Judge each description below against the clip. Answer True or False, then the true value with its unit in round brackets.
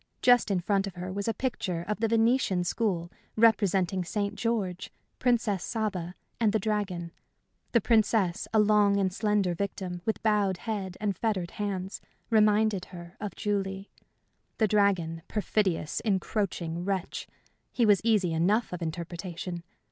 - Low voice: False (200 Hz)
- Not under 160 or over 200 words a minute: False (145 wpm)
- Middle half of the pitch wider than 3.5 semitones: False (3.1 semitones)